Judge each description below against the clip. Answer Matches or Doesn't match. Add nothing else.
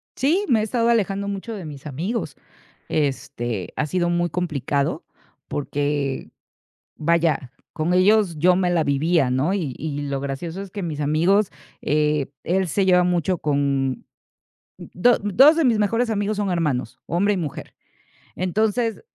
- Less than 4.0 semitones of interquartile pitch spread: Doesn't match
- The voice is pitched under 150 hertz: Doesn't match